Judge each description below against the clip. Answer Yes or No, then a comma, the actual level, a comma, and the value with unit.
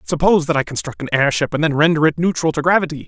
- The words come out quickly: Yes, fast, 255 wpm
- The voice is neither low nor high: Yes, medium, 155 Hz